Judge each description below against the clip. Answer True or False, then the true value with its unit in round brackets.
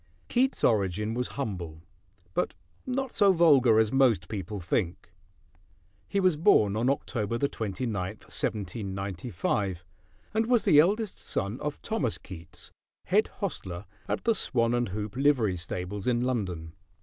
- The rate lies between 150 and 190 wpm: False (135 wpm)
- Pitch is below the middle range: True (110 Hz)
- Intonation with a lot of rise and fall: True (6.5 semitones)